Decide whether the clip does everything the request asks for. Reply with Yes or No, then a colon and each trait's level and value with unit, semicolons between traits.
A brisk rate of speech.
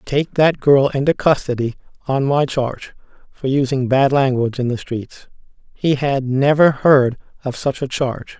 No: average, 165 wpm